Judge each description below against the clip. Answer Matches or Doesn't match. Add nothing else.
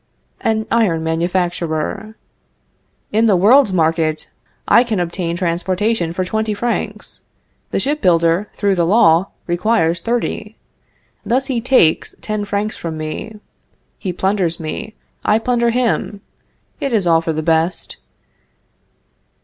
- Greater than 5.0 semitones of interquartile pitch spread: Doesn't match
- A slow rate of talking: Matches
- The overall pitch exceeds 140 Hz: Matches